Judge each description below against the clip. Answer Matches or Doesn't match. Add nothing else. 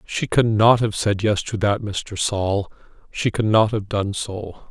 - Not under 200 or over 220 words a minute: Doesn't match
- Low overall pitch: Matches